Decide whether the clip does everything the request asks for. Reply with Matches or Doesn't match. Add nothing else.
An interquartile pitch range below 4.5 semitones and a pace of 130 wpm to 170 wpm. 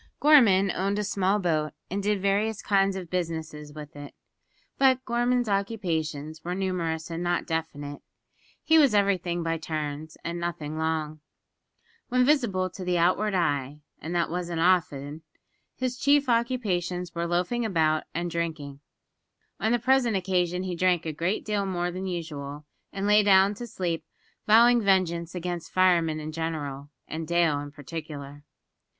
Matches